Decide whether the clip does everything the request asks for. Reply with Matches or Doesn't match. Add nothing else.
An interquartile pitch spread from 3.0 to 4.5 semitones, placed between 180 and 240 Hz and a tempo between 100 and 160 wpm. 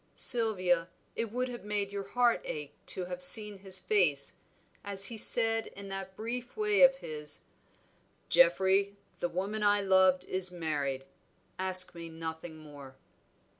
Matches